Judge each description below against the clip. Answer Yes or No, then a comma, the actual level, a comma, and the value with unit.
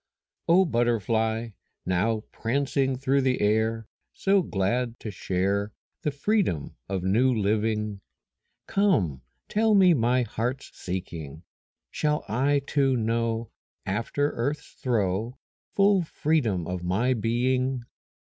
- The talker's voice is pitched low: Yes, low, 115 Hz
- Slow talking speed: Yes, slow, 110 wpm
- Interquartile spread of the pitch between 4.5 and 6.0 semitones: Yes, average, 5.0 semitones